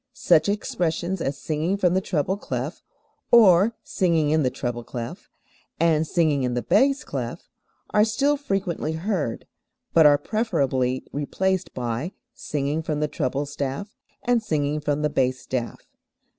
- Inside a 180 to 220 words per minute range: No, average, 145 wpm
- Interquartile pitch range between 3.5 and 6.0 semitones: Yes, average, 5.2 semitones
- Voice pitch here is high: No, medium, 155 Hz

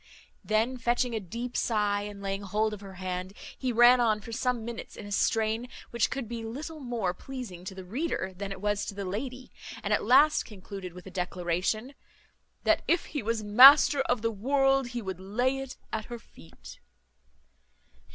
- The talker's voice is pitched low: No, high, 220 Hz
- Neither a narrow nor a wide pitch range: Yes, average, 4.1 semitones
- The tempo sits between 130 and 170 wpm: No, average, 190 wpm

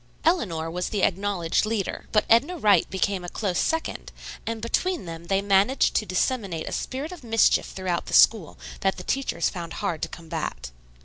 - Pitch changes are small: No, average, 4.7 semitones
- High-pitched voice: Yes, high, 200 Hz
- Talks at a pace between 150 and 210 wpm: Yes, average, 180 wpm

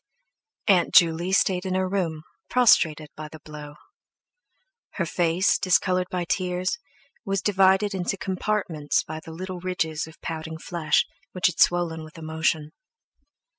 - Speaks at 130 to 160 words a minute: Yes, slow, 135 wpm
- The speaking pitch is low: No, medium, 175 Hz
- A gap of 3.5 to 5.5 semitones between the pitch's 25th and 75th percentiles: No, average, 2.8 semitones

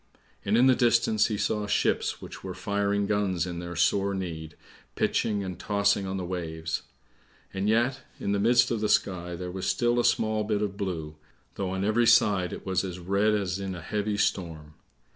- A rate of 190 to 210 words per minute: Yes, average, 200 wpm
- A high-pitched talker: No, low, 100 Hz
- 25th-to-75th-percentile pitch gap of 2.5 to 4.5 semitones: Yes, average, 2.9 semitones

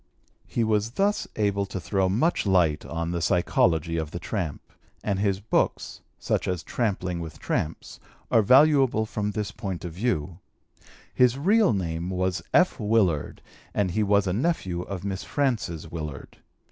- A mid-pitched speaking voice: No, low, 100 Hz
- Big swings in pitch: No, average, 4.3 semitones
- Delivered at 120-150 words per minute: No, average, 160 wpm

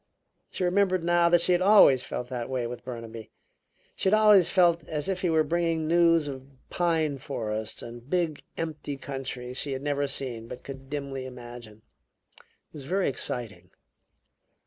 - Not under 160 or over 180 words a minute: Yes, average, 170 wpm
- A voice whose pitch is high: No, medium, 140 Hz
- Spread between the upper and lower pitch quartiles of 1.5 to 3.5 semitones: No, wide, 5.5 semitones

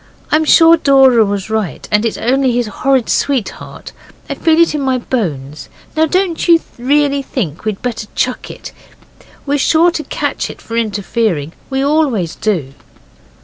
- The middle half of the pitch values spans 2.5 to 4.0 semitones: No, wide, 5.6 semitones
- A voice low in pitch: No, very high, 255 Hz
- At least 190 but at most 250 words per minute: No, average, 160 wpm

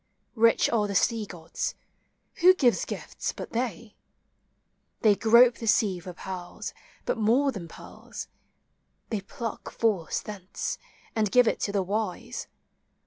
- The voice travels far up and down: No, average, 3.3 semitones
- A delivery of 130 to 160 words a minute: Yes, average, 140 wpm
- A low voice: No, high, 215 Hz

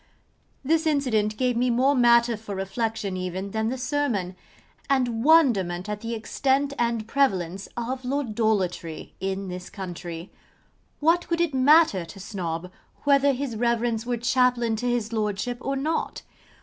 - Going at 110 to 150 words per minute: Yes, average, 145 wpm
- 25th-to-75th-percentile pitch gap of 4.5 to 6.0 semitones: Yes, average, 5.1 semitones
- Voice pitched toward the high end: Yes, high, 235 Hz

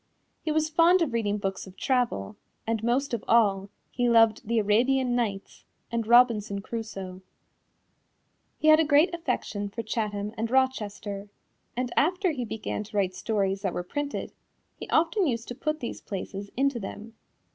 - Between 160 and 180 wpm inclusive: Yes, average, 165 wpm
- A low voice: No, high, 230 Hz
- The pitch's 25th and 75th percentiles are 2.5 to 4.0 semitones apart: No, average, 4.6 semitones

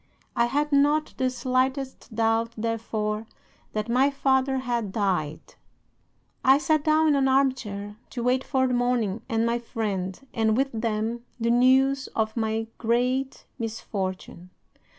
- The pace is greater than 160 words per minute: No, average, 145 wpm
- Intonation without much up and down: No, average, 3.3 semitones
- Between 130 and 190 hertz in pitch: No, high, 235 Hz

